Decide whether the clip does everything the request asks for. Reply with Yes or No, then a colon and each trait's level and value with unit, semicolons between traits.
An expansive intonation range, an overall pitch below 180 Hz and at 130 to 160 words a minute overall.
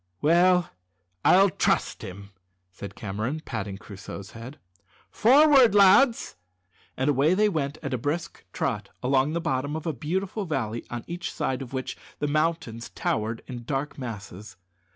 Yes: wide, 6.9 semitones; medium, 140 Hz; average, 150 wpm